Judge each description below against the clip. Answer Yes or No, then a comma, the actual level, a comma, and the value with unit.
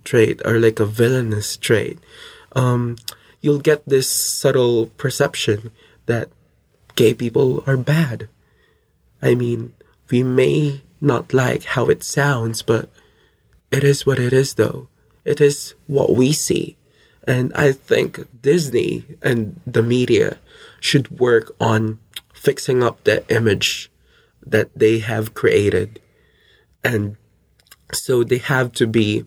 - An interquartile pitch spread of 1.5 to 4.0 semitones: Yes, average, 3.5 semitones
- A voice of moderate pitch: No, low, 125 Hz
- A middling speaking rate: No, slow, 125 wpm